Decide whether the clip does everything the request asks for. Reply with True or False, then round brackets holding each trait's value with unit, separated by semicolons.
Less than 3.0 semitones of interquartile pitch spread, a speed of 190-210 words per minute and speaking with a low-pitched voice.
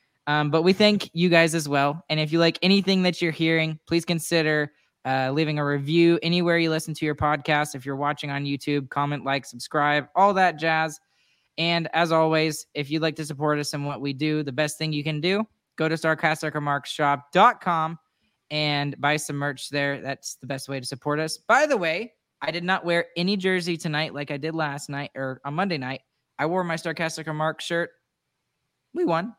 False (2.4 semitones; 205 wpm; 155 Hz)